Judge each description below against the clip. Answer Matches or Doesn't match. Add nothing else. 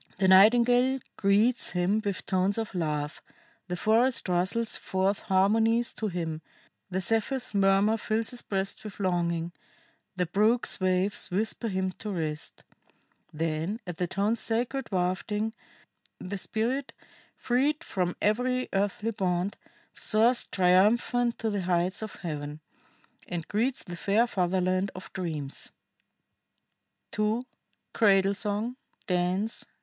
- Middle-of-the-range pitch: Doesn't match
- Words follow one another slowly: Matches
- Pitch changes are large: Doesn't match